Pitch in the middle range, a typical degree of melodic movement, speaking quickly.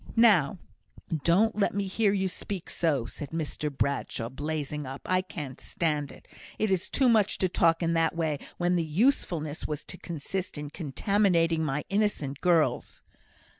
No: medium, 165 Hz; average, 4.4 semitones; average, 165 wpm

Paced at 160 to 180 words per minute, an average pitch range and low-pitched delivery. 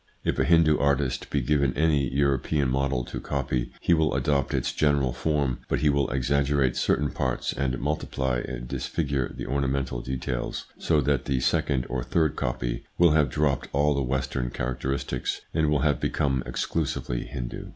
No: average, 170 wpm; narrow, 2.3 semitones; very low, 70 Hz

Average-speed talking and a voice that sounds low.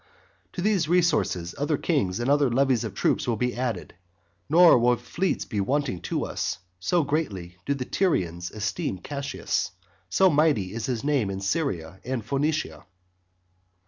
Yes: average, 155 wpm; low, 125 Hz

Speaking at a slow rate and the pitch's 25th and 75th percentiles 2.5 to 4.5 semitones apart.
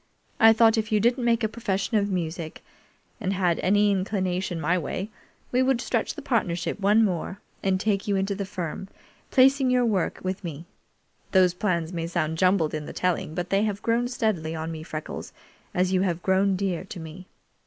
No: average, 195 wpm; average, 3.7 semitones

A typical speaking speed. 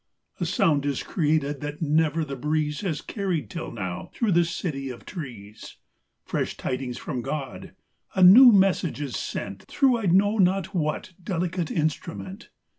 Yes: average, 160 wpm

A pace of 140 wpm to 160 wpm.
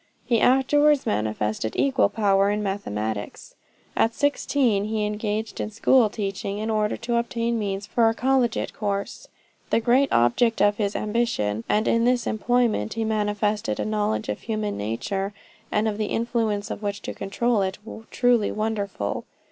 Yes: average, 150 wpm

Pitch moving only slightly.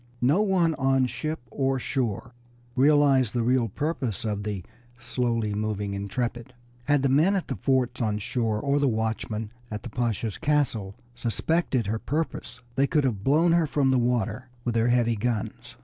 No: average, 4.0 semitones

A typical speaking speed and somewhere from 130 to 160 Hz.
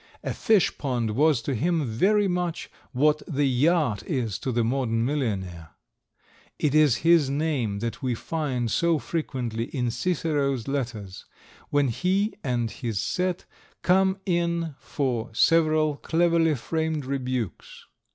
No: slow, 130 wpm; medium, 140 Hz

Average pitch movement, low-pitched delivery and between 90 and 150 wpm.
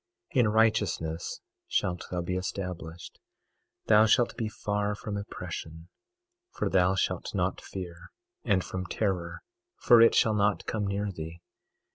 Yes: average, 3.2 semitones; very low, 95 Hz; average, 140 wpm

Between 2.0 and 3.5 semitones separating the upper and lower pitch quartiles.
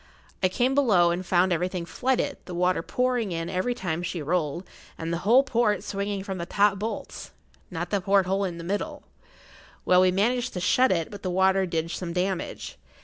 Yes: average, 2.9 semitones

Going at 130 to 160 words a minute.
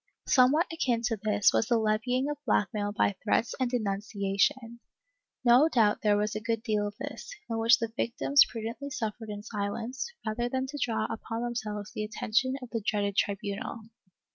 No: average, 175 wpm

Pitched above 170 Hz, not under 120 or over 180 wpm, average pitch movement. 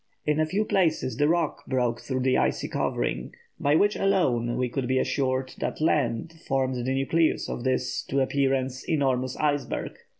No: low, 135 Hz; average, 170 wpm; average, 3.0 semitones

